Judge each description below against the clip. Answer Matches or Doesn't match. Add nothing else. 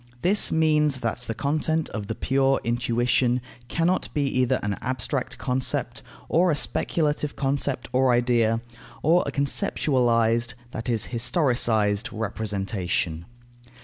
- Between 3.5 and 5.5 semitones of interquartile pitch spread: Matches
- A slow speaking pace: Matches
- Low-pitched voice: Matches